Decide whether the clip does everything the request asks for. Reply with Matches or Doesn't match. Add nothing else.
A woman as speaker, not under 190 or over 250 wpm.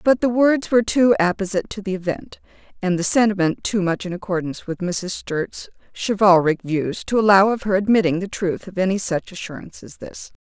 Matches